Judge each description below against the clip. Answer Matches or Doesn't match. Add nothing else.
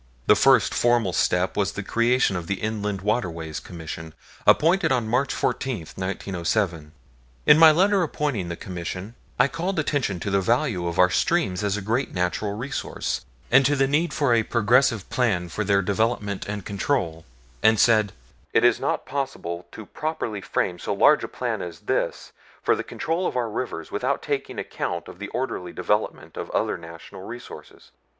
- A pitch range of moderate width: Doesn't match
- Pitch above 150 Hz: Doesn't match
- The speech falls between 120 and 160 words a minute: Doesn't match